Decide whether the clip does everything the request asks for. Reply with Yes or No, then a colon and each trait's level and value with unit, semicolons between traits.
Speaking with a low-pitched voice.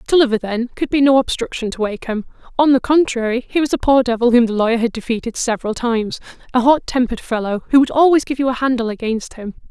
No: high, 245 Hz